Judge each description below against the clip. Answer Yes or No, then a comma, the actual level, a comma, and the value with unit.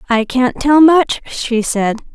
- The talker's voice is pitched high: Yes, very high, 255 Hz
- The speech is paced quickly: No, average, 170 wpm